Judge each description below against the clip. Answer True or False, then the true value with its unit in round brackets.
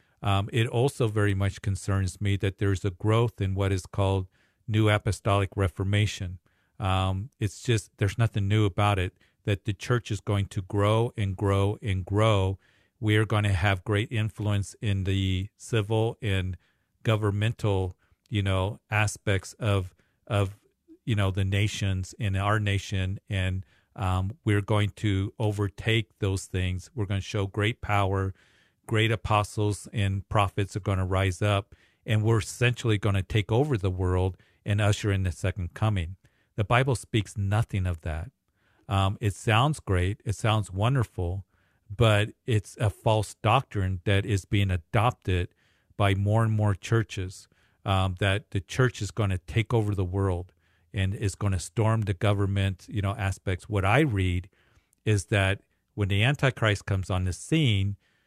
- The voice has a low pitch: True (100 Hz)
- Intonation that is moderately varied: False (2.1 semitones)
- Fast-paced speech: False (165 wpm)